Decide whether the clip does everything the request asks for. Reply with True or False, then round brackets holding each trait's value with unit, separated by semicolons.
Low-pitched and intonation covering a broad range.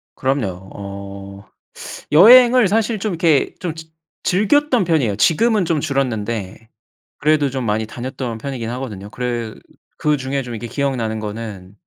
True (130 Hz; 6.8 semitones)